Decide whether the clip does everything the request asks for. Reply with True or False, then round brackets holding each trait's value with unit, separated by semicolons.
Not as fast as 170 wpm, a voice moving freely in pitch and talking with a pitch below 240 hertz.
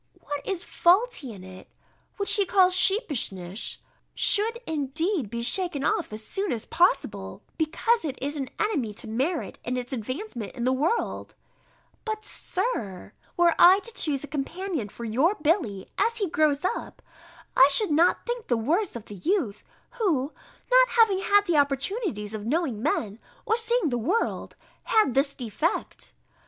False (160 wpm; 8.3 semitones; 305 Hz)